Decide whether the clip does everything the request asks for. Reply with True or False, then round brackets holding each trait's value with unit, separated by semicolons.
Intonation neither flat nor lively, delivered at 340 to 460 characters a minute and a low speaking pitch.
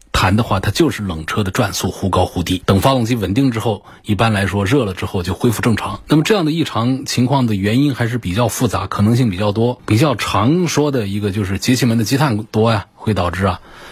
True (4.1 semitones; 350 characters per minute; 110 Hz)